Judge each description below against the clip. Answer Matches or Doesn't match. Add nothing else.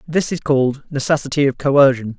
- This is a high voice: Doesn't match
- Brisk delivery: Doesn't match